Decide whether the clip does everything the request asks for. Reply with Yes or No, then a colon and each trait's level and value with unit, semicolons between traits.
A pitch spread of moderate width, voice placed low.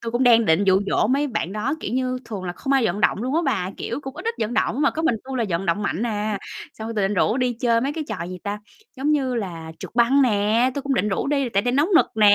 No: average, 4.6 semitones; high, 230 Hz